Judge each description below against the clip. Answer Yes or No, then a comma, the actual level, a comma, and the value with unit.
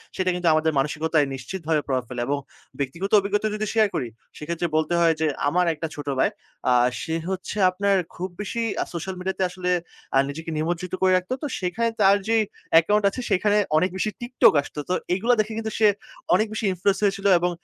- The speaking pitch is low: No, medium, 185 Hz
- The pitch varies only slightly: No, average, 4.1 semitones